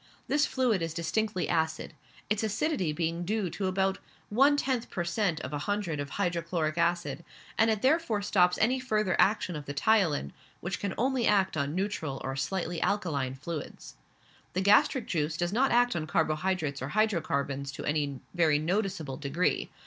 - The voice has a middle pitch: Yes, medium, 180 Hz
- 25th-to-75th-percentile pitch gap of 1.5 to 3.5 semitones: No, average, 5.3 semitones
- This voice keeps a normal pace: Yes, average, 170 wpm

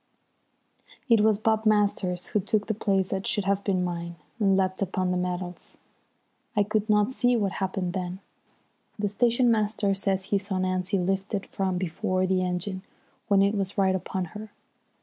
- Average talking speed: Yes, average, 170 wpm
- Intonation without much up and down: Yes, narrow, 2.1 semitones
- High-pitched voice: Yes, high, 195 Hz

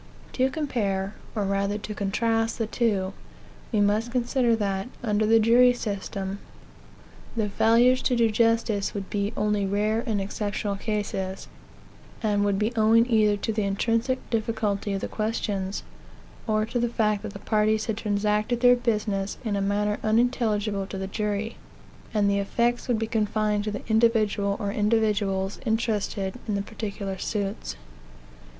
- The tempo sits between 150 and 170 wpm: Yes, average, 155 wpm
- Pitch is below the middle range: No, high, 210 Hz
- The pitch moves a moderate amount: No, narrow, 2.1 semitones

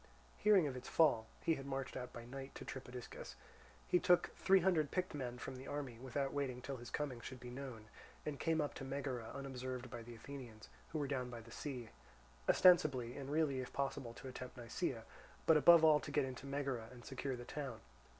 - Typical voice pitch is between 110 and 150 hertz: Yes, low, 135 Hz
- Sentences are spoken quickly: Yes, fast, 210 wpm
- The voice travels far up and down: No, average, 2.7 semitones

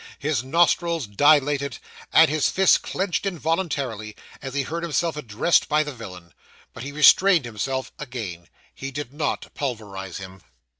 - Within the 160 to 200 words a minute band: No, average, 145 wpm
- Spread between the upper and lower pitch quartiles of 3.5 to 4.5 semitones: No, wide, 5.6 semitones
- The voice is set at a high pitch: No, medium, 140 Hz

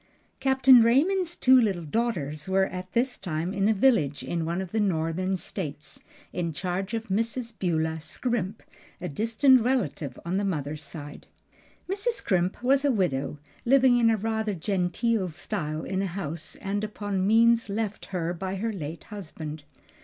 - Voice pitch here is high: Yes, high, 195 Hz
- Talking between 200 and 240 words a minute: No, average, 160 wpm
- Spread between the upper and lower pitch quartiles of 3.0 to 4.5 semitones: No, wide, 5.5 semitones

